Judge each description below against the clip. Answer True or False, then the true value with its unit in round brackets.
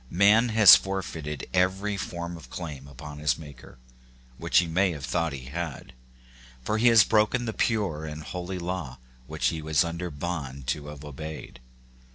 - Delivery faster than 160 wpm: True (170 wpm)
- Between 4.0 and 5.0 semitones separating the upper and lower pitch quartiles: True (4.3 semitones)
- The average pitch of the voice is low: True (85 Hz)